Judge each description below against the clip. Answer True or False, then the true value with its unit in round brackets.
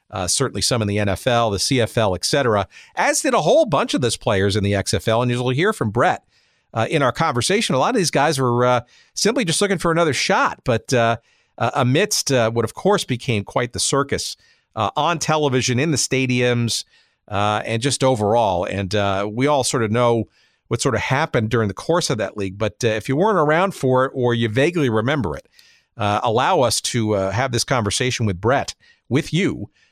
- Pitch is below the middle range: True (120 Hz)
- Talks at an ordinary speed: False (215 wpm)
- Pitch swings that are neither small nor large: True (3.8 semitones)